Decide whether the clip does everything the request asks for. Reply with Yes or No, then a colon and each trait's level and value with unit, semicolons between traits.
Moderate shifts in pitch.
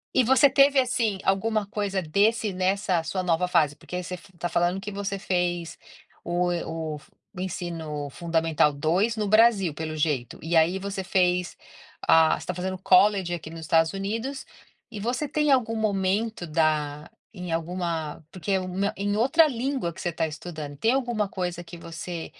Yes: average, 4.1 semitones